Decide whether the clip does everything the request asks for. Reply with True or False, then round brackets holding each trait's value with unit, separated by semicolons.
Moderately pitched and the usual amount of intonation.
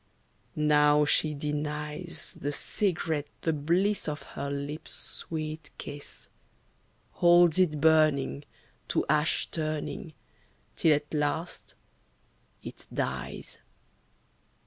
False (150 Hz; 1.6 semitones)